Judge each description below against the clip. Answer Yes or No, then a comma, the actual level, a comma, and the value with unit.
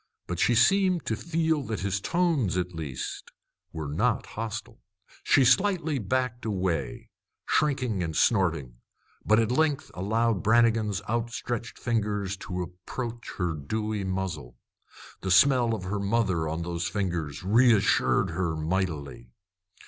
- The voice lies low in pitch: Yes, low, 105 Hz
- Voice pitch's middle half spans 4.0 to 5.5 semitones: Yes, average, 5.1 semitones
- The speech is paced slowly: Yes, slow, 130 wpm